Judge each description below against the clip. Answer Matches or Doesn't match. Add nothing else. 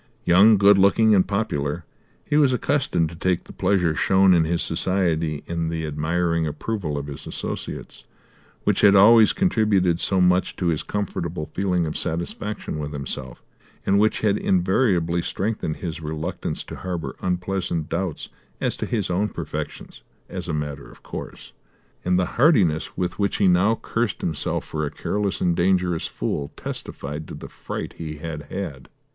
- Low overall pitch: Matches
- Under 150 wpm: Doesn't match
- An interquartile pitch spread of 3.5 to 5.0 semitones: Matches